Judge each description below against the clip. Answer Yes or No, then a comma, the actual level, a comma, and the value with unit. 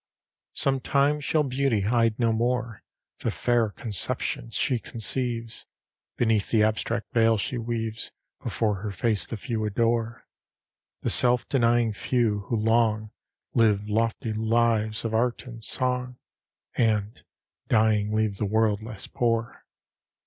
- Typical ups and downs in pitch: No, narrow, 1.9 semitones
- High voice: No, low, 115 Hz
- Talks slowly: Yes, slow, 130 wpm